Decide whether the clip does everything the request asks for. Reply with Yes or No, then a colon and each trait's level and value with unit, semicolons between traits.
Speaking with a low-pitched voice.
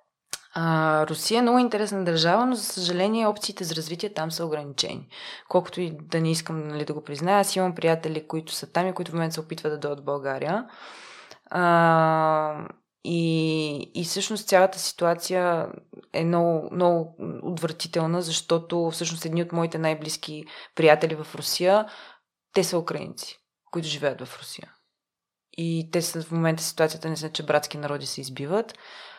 No: medium, 165 Hz